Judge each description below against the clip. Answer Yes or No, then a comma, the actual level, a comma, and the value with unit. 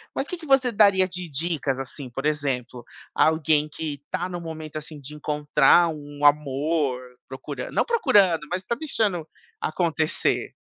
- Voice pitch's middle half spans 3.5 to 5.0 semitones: Yes, average, 3.8 semitones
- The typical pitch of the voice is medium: Yes, medium, 155 Hz